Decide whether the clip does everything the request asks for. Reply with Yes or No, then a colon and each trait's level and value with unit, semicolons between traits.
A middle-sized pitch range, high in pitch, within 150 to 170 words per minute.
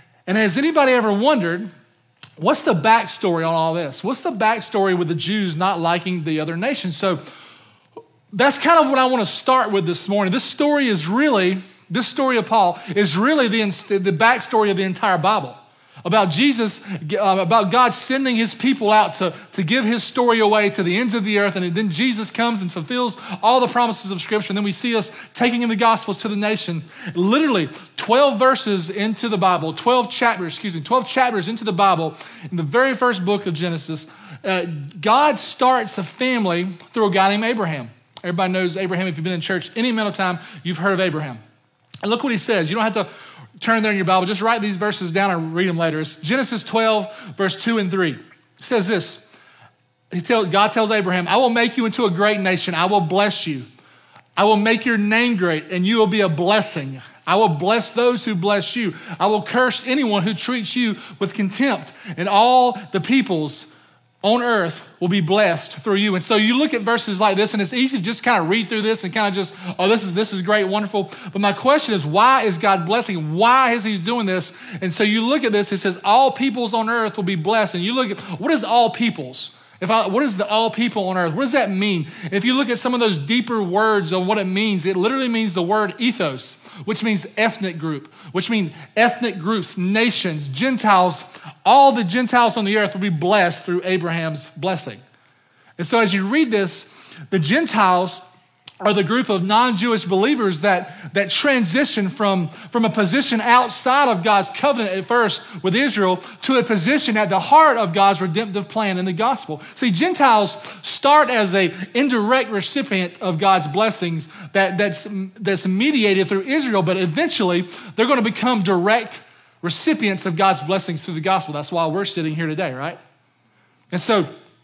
No: average, 4.2 semitones; high, 205 Hz; fast, 205 wpm